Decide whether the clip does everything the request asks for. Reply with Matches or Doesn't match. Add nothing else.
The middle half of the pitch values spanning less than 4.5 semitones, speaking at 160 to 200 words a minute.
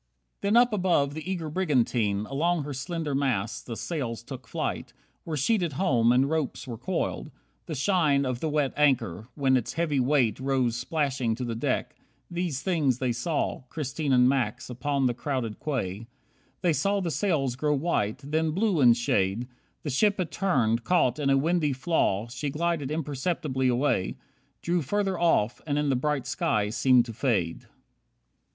Doesn't match